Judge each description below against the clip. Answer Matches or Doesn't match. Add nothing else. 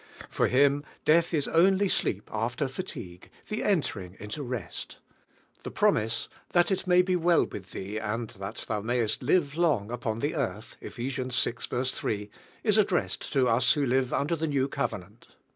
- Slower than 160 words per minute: Doesn't match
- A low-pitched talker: Matches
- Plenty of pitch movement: Matches